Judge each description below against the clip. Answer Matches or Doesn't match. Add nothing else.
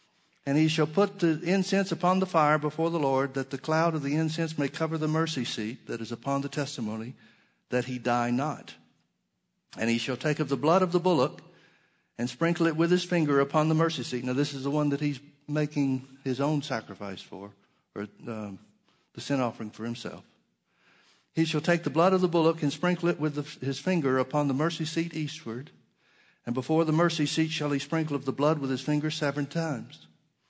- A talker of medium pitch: Matches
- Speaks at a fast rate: Matches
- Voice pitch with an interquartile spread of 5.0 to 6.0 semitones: Doesn't match